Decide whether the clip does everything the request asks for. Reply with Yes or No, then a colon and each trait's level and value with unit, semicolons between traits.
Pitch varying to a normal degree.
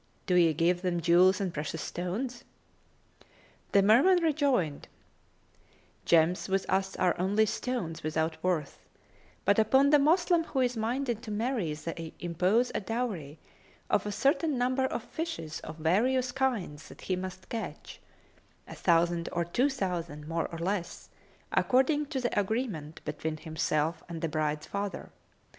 No: wide, 7.0 semitones